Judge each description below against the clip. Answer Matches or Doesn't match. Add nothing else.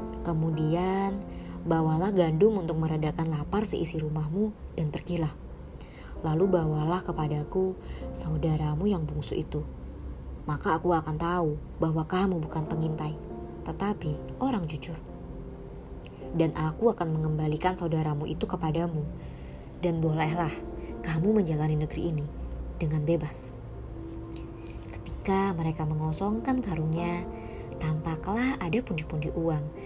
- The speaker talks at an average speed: Matches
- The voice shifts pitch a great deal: Doesn't match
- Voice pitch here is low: Doesn't match